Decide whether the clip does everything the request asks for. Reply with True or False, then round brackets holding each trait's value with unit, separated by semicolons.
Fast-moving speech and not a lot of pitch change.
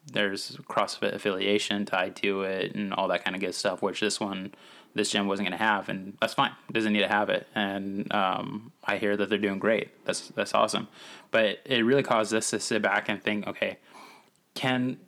True (210 wpm; 1.3 semitones)